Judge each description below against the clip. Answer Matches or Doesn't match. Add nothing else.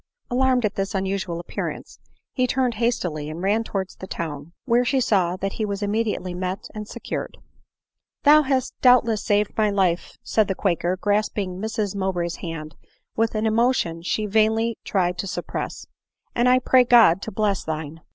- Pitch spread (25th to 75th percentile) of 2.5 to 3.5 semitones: Doesn't match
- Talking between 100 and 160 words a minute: Doesn't match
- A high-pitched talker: Matches